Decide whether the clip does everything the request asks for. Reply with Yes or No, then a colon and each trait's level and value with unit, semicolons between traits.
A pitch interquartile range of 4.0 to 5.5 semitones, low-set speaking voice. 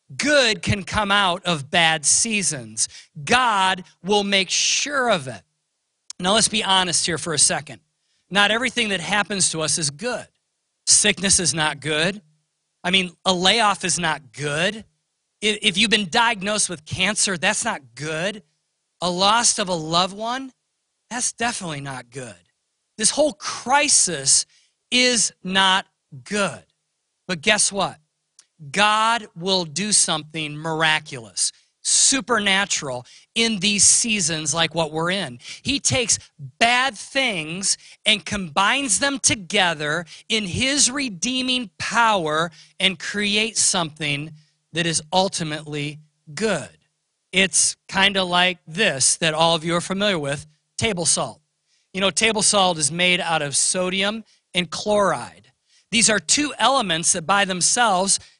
No: average, 5.0 semitones; medium, 185 Hz